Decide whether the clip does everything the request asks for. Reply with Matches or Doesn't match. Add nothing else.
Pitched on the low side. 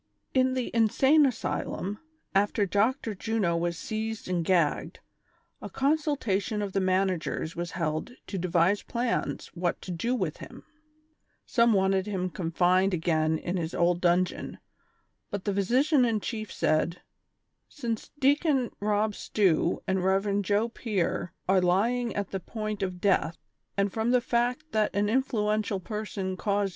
Doesn't match